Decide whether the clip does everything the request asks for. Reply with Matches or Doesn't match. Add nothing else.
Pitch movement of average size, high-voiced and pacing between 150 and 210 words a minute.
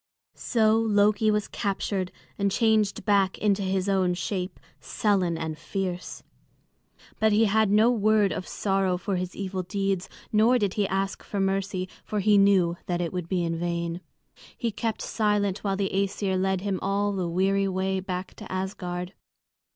Doesn't match